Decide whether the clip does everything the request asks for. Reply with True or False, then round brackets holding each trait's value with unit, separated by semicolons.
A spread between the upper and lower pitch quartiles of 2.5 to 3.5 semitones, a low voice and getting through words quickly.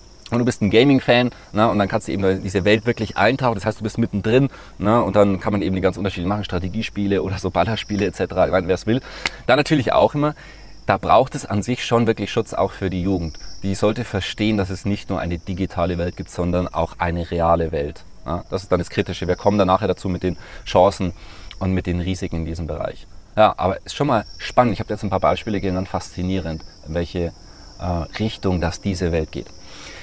True (3.1 semitones; 95 Hz; 225 wpm)